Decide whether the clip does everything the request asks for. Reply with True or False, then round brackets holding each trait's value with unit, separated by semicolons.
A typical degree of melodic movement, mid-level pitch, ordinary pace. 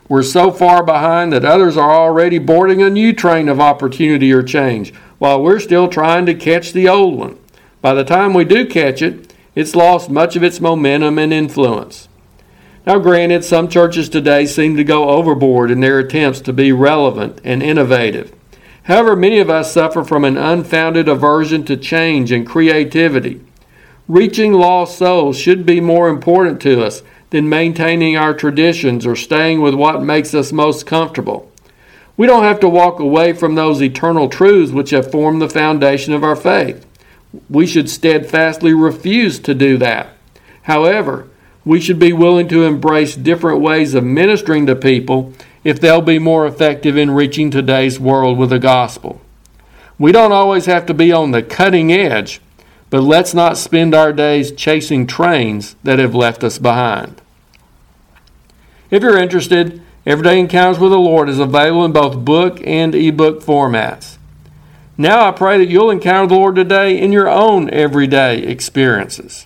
True (3.8 semitones; 155 Hz; 170 wpm)